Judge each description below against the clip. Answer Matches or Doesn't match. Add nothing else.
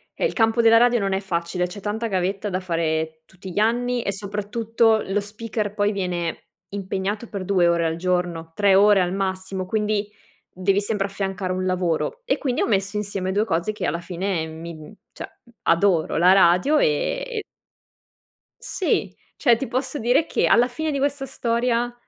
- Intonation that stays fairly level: Doesn't match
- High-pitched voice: Matches